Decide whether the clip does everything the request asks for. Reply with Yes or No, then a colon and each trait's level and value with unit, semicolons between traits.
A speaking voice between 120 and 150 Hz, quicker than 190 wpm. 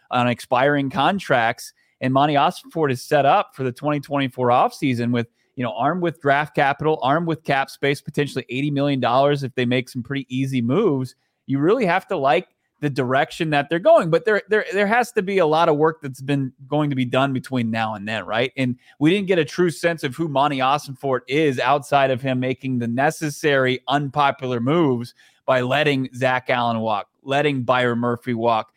Yes: low, 135 Hz; average, 200 wpm